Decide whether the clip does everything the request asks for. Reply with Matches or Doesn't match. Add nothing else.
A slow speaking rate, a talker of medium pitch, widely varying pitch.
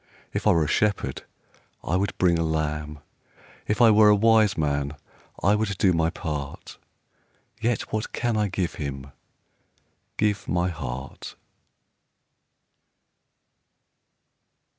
Doesn't match